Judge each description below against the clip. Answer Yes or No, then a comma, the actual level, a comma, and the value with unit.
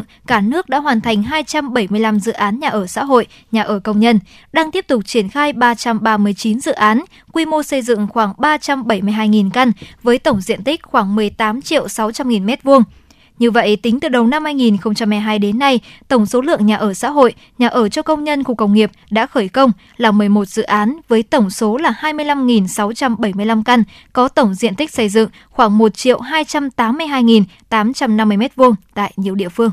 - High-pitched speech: Yes, high, 230 Hz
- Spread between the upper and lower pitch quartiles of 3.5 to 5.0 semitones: Yes, average, 3.8 semitones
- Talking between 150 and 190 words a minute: Yes, average, 180 wpm